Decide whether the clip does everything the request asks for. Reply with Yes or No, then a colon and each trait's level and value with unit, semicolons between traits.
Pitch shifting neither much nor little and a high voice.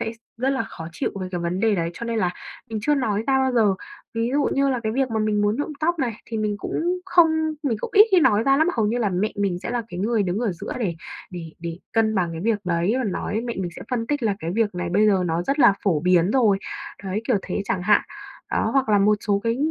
Yes: average, 4.7 semitones; high, 215 Hz